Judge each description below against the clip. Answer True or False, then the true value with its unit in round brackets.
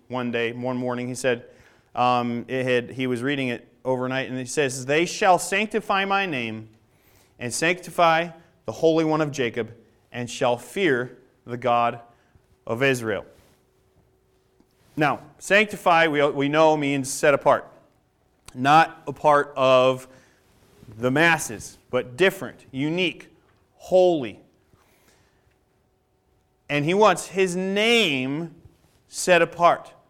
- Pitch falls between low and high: False (130 Hz)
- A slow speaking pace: True (120 wpm)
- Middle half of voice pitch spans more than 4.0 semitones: True (5.3 semitones)